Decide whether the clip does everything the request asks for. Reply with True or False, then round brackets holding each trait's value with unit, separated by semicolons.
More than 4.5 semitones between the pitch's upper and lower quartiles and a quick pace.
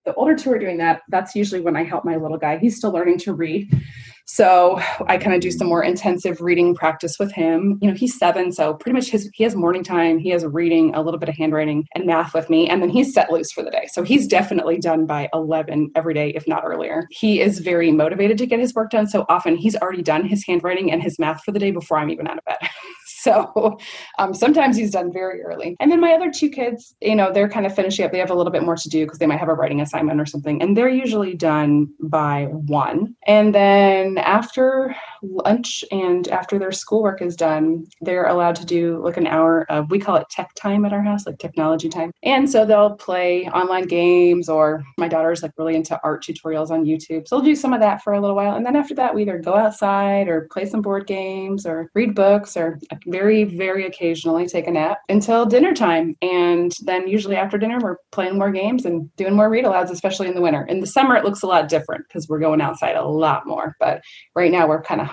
False (4.1 semitones; 245 wpm)